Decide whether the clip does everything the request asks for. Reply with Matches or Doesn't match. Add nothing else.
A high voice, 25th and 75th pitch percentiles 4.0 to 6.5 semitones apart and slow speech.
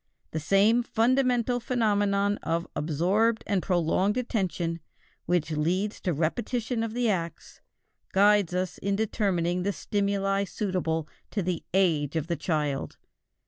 Matches